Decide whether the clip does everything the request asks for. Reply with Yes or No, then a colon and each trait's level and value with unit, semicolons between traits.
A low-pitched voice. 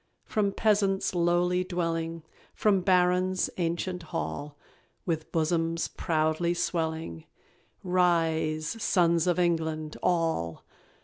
No: medium, 170 Hz